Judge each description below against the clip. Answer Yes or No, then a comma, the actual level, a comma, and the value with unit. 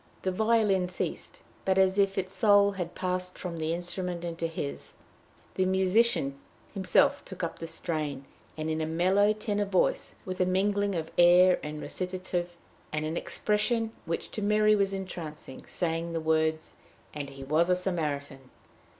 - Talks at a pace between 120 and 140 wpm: No, average, 160 wpm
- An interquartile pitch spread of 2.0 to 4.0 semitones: Yes, average, 3.3 semitones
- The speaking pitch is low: No, medium, 180 Hz